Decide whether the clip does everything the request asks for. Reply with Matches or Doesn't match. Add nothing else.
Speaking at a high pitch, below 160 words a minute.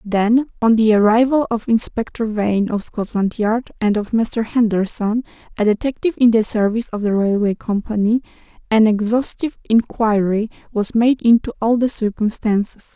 Matches